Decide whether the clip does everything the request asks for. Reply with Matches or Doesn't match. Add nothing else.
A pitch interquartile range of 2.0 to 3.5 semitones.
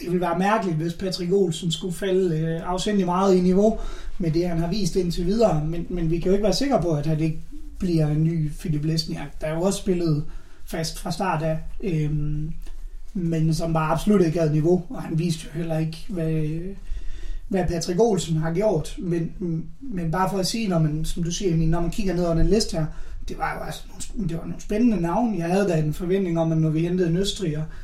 Matches